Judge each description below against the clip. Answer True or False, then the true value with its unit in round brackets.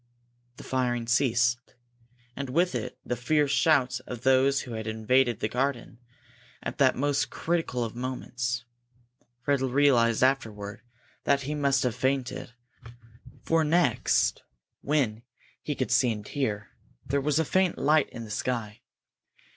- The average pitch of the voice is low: True (130 Hz)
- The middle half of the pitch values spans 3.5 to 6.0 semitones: False (2.9 semitones)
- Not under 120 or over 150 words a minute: True (140 wpm)